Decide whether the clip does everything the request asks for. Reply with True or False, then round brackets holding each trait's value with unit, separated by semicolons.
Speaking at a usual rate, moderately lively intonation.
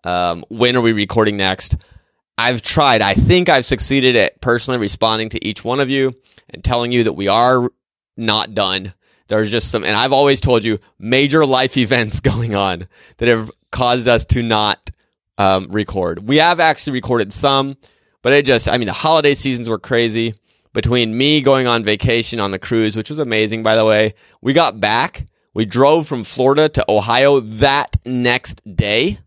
True (185 wpm; 3.4 semitones)